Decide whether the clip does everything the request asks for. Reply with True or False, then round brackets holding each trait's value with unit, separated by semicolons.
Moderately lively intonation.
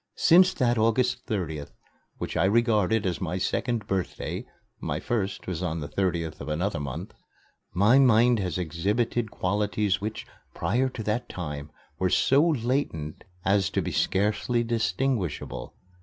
True (4.9 semitones)